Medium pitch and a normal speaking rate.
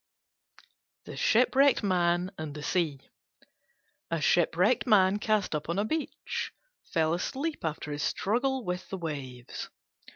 No: medium, 180 Hz; slow, 130 wpm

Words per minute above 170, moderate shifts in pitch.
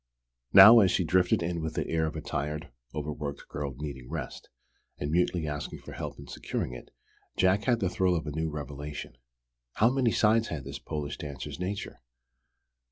Yes: average, 180 wpm; average, 4.1 semitones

